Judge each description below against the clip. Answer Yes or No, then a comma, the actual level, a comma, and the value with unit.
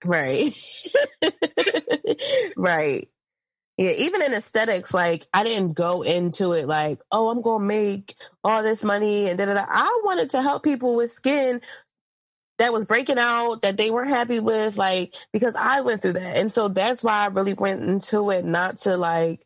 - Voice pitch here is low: No, high, 215 Hz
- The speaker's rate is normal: Yes, average, 175 wpm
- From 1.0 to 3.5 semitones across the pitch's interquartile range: No, average, 4.4 semitones